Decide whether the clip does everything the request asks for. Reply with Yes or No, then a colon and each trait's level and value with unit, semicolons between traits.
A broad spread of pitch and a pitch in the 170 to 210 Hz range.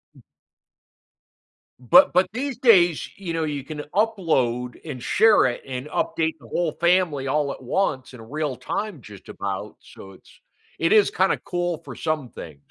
No: wide, 6.3 semitones; medium, 155 Hz